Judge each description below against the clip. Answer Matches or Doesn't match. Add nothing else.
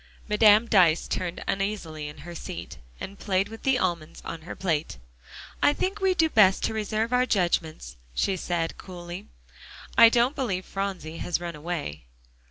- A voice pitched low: Doesn't match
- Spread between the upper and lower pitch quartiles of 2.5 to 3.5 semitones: Doesn't match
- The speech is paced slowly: Doesn't match